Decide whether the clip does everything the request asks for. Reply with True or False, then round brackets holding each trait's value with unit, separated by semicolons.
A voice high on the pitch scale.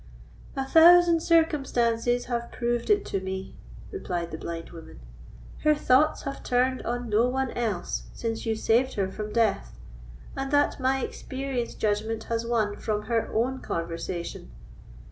True (235 Hz)